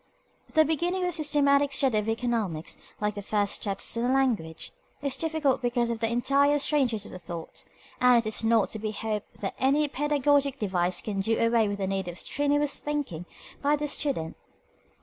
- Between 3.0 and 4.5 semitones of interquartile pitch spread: No, wide, 5.5 semitones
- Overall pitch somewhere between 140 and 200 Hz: No, high, 240 Hz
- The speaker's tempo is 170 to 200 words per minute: Yes, average, 190 wpm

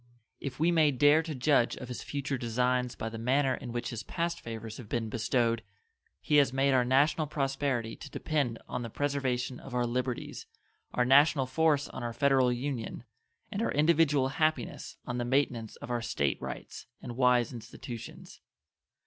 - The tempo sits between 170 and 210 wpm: Yes, average, 175 wpm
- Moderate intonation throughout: Yes, average, 3.1 semitones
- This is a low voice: Yes, low, 130 Hz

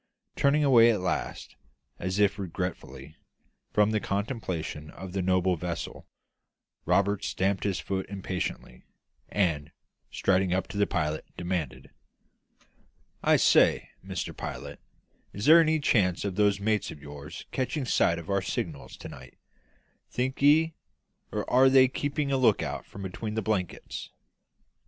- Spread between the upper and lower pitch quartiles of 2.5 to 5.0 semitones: Yes, average, 4.5 semitones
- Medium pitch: No, low, 100 Hz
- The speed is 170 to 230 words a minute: No, average, 140 wpm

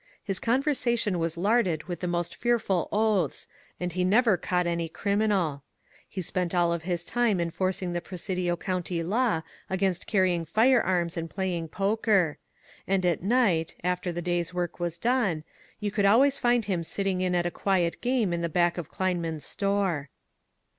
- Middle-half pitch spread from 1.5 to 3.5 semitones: Yes, average, 3.1 semitones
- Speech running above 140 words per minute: Yes, average, 170 wpm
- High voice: No, medium, 180 Hz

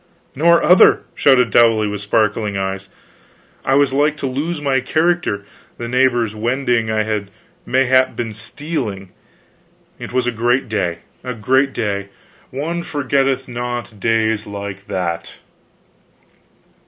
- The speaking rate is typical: No, slow, 130 wpm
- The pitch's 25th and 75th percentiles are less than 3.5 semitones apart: No, average, 4.2 semitones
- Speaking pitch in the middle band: No, low, 120 Hz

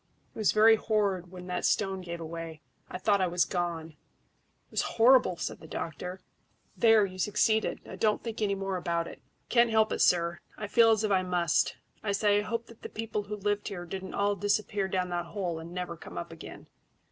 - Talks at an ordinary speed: No, fast, 215 wpm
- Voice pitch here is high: Yes, high, 195 Hz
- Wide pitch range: No, average, 3.3 semitones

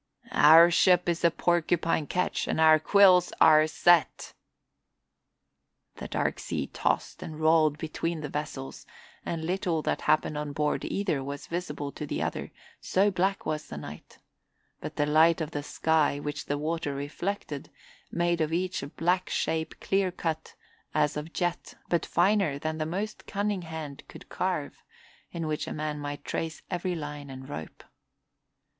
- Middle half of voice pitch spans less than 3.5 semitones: Yes, average, 2.7 semitones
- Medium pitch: Yes, medium, 160 Hz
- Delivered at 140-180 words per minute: Yes, average, 160 wpm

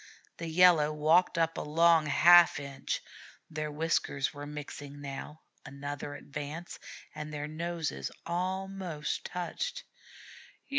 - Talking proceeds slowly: Yes, slow, 110 wpm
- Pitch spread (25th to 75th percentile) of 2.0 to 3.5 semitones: Yes, average, 2.7 semitones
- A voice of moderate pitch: Yes, medium, 155 Hz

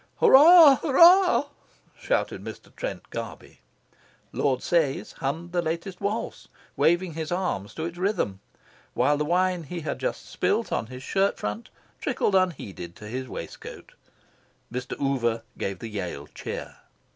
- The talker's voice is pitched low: No, medium, 165 Hz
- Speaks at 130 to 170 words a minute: Yes, average, 140 wpm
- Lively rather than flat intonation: Yes, wide, 7.0 semitones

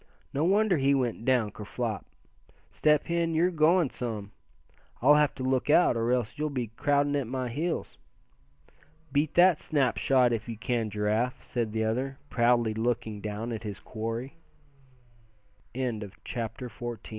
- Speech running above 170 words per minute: No, average, 150 wpm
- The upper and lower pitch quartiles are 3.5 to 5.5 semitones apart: Yes, average, 4.2 semitones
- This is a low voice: Yes, low, 125 Hz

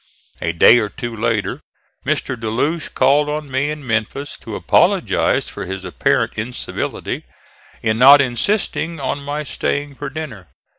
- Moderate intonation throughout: Yes, average, 4.6 semitones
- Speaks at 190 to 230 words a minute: No, average, 150 wpm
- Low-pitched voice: Yes, low, 130 Hz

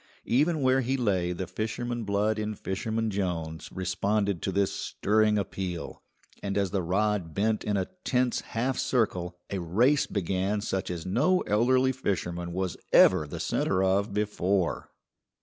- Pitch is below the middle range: Yes, low, 100 Hz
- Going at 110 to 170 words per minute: Yes, average, 150 wpm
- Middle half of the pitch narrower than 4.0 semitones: Yes, average, 3.4 semitones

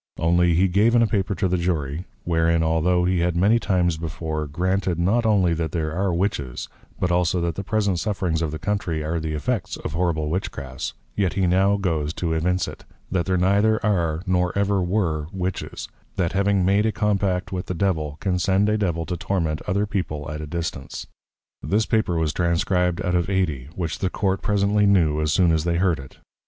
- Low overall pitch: Yes, very low, 90 Hz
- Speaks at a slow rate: No, fast, 205 wpm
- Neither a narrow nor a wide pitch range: Yes, average, 3.1 semitones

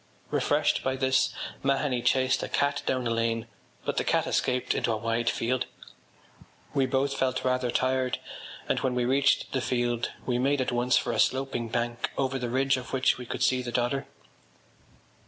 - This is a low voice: Yes, low, 130 Hz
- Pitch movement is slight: Yes, narrow, 1.6 semitones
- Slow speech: No, average, 185 wpm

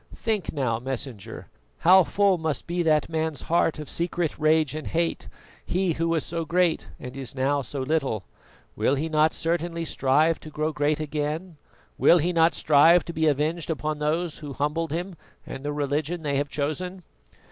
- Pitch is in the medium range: Yes, medium, 155 Hz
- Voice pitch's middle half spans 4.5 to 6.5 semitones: No, narrow, 2.5 semitones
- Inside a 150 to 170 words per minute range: No, average, 180 wpm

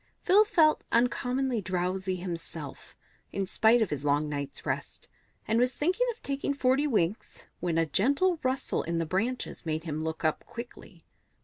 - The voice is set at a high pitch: Yes, high, 210 Hz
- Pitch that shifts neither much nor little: No, wide, 8.1 semitones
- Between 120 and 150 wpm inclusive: No, average, 165 wpm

